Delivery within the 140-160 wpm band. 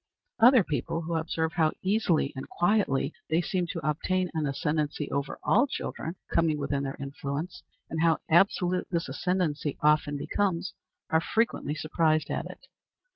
Yes: average, 150 wpm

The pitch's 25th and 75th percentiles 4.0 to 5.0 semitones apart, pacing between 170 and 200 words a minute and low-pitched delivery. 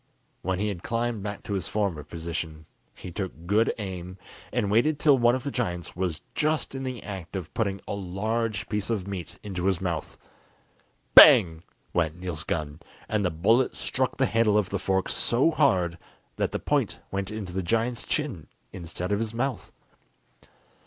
Yes: average, 4.5 semitones; average, 180 wpm; low, 100 Hz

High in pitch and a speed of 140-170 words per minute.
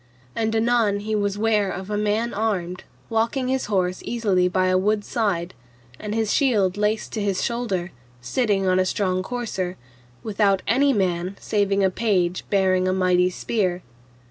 Yes: high, 200 Hz; average, 165 wpm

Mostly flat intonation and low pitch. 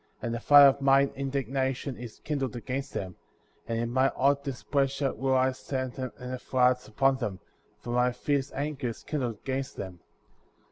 Yes: narrow, 1.9 semitones; low, 130 Hz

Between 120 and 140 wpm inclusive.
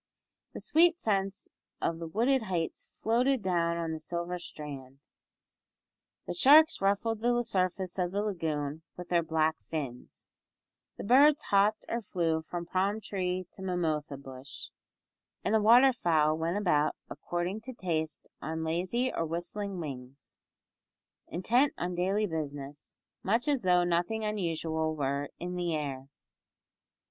Yes: slow, 135 wpm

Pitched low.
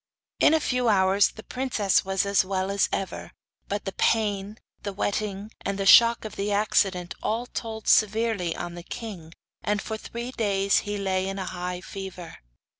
No: high, 200 Hz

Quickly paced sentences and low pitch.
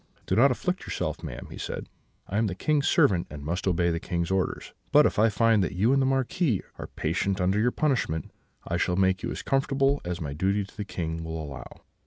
Yes: fast, 230 wpm; very low, 95 Hz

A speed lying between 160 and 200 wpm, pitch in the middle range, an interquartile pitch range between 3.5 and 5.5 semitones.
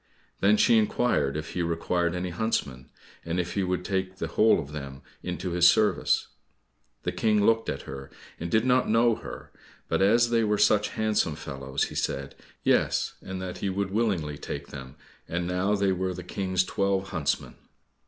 No: average, 185 wpm; very low, 95 Hz; average, 4.1 semitones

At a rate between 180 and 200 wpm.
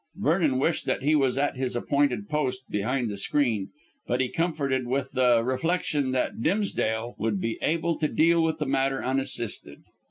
No: average, 170 wpm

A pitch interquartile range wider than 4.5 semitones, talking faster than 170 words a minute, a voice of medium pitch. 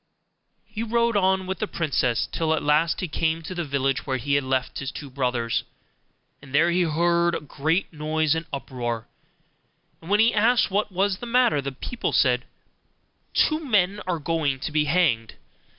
Yes: wide, 5.4 semitones; average, 180 wpm; medium, 160 Hz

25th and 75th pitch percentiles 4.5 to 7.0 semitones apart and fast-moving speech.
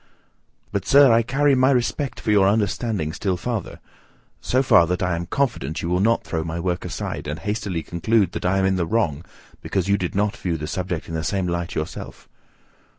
Yes: average, 4.9 semitones; fast, 210 wpm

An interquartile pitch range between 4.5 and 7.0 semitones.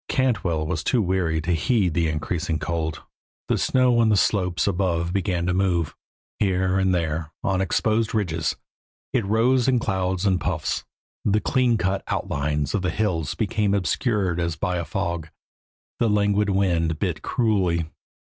No: average, 3.8 semitones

